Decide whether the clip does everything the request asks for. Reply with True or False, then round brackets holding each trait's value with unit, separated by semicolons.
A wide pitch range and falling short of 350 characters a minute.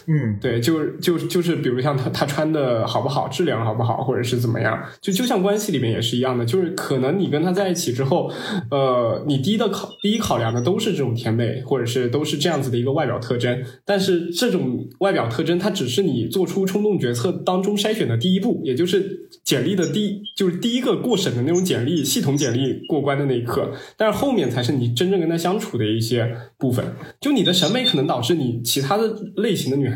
False (7.5 semitones; 355 characters per minute)